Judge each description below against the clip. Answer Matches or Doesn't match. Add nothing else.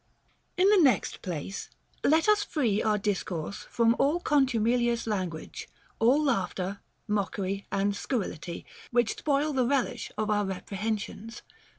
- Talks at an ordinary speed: Doesn't match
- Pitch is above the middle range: Matches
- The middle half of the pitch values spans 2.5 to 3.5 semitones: Doesn't match